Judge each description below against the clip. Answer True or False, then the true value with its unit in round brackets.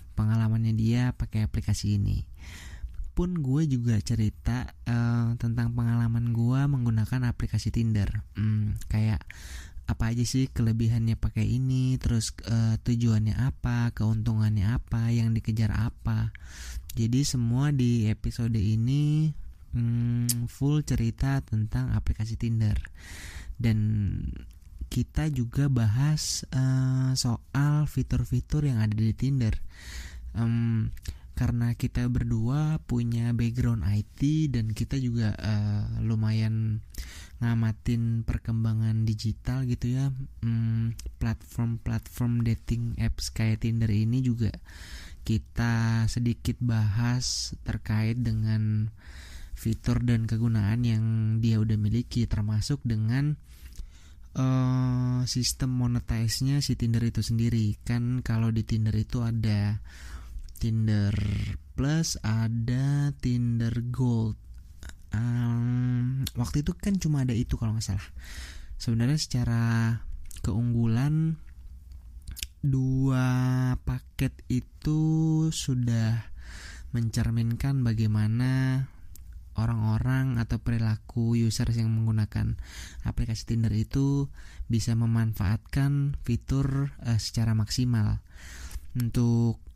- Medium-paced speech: False (100 wpm)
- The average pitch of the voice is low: True (115 Hz)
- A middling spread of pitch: False (2.3 semitones)